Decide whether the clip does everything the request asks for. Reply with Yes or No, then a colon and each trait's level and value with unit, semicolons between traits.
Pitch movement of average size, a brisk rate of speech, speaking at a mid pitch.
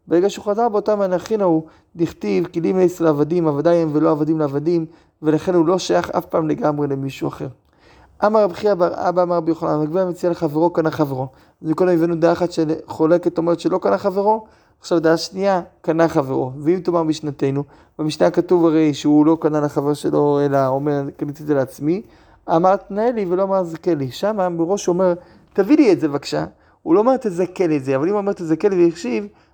Yes: average, 3.4 semitones; fast, 170 wpm; medium, 170 Hz